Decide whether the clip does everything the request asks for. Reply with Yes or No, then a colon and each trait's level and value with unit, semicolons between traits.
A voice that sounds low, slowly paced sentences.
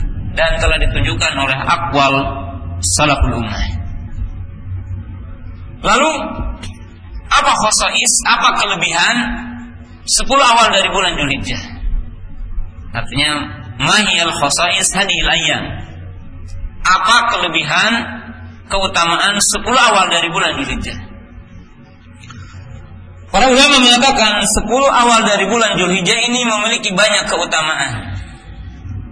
Yes: low, 110 Hz; slow, 85 wpm